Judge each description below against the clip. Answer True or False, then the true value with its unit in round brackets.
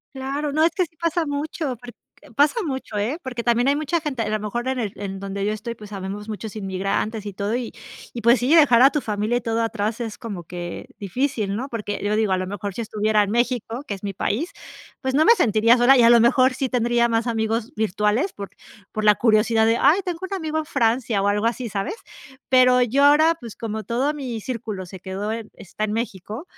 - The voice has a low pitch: False (230 Hz)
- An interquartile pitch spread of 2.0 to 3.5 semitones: False (4.0 semitones)